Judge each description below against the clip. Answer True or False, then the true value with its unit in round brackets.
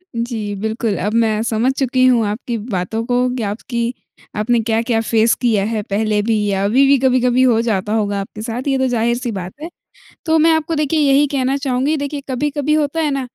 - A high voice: True (235 Hz)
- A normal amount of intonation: True (3.7 semitones)